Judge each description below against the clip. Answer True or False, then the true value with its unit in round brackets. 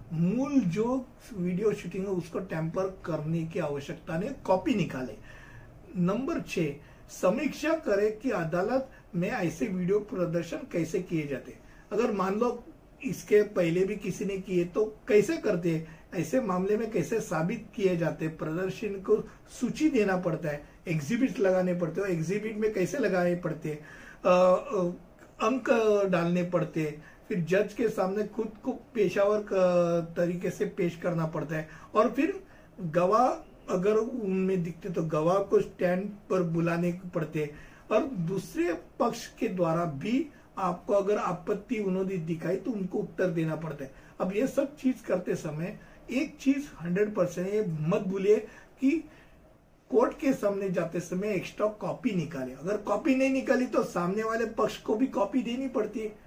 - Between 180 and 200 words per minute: False (155 wpm)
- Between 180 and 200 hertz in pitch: True (190 Hz)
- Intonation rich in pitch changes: False (4.0 semitones)